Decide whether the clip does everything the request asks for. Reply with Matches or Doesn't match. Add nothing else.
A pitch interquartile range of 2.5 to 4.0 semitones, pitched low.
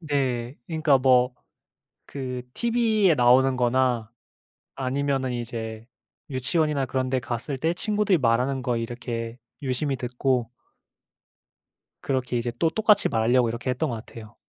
Matches